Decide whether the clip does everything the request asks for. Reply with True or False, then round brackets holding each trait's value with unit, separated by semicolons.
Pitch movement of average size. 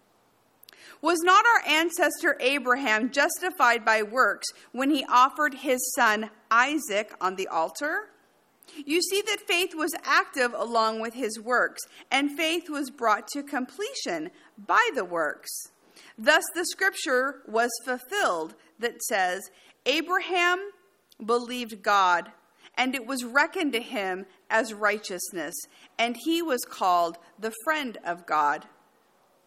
False (6.9 semitones)